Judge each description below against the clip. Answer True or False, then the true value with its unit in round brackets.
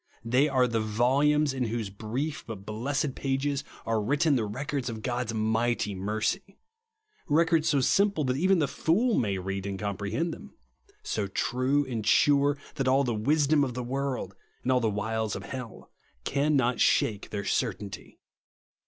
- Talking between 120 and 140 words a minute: False (170 wpm)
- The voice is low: True (125 Hz)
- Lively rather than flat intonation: False (4.9 semitones)